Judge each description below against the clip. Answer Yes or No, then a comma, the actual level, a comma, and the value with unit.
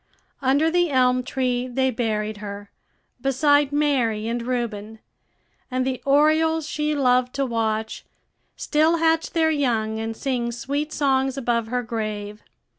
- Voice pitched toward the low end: No, very high, 255 Hz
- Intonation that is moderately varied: Yes, average, 4.3 semitones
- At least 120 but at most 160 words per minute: Yes, slow, 135 wpm